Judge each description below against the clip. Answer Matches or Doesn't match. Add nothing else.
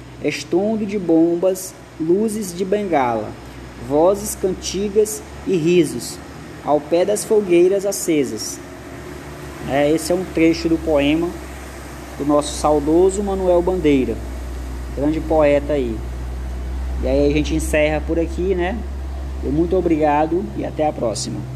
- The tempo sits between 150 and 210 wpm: Doesn't match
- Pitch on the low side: Doesn't match